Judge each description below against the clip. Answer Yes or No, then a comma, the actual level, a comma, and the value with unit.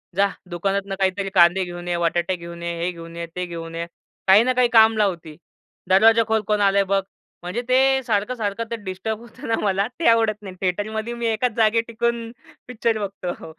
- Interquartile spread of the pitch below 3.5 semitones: No, average, 4.1 semitones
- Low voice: No, high, 200 Hz